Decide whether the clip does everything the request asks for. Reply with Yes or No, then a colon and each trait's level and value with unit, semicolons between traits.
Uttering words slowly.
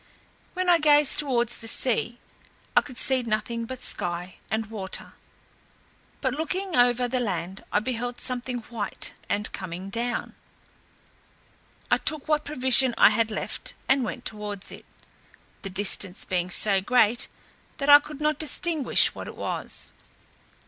No: average, 145 wpm